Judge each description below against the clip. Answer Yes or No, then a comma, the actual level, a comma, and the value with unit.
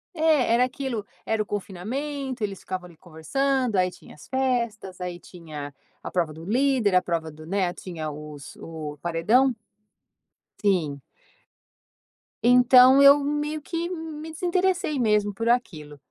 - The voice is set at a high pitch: Yes, high, 215 Hz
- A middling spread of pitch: No, wide, 7.8 semitones